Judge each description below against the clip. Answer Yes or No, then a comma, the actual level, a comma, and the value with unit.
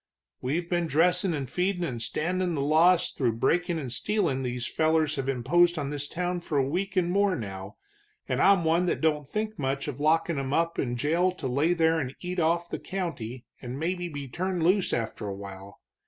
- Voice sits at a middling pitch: Yes, medium, 160 Hz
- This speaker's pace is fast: Yes, fast, 210 wpm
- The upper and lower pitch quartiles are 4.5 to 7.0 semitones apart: Yes, average, 4.8 semitones